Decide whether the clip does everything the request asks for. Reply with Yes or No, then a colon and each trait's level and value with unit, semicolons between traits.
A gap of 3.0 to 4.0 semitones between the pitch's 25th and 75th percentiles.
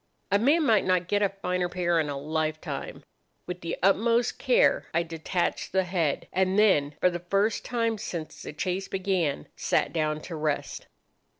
Yes: average, 3.7 semitones